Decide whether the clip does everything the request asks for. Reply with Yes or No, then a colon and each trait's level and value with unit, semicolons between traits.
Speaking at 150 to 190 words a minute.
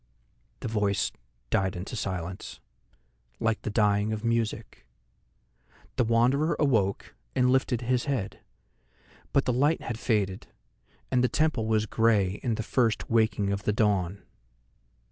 No: slow, 135 wpm